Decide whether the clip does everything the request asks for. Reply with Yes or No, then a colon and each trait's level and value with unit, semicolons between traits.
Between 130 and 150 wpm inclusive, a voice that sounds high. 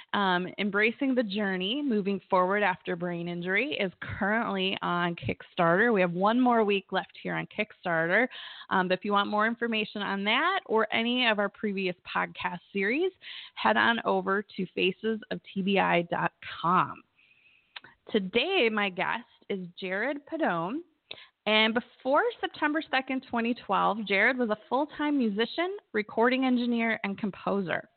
Yes: slow, 135 wpm; high, 215 Hz